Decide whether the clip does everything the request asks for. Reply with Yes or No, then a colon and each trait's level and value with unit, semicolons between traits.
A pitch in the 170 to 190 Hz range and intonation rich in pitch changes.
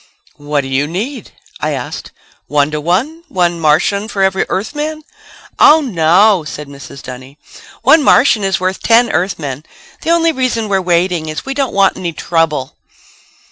Yes: medium, 185 Hz; wide, 7.3 semitones